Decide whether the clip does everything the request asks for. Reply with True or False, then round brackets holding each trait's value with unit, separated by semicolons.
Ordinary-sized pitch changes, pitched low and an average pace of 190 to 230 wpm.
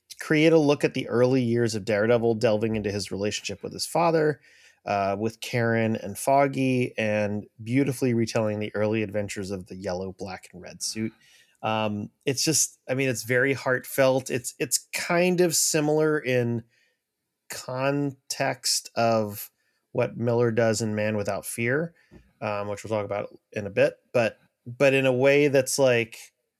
False (4.2 semitones; 120 Hz; 160 wpm)